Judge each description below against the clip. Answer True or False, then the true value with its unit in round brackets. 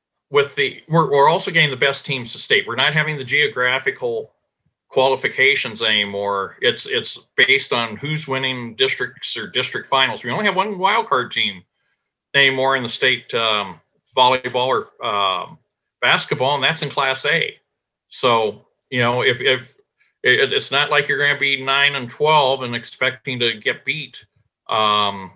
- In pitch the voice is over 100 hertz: True (135 Hz)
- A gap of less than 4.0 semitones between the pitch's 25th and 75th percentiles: False (4.3 semitones)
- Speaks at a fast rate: False (165 wpm)